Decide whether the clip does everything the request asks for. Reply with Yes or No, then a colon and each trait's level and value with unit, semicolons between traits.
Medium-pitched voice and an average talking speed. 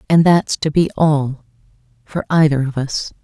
Yes: medium, 150 Hz; average, 150 wpm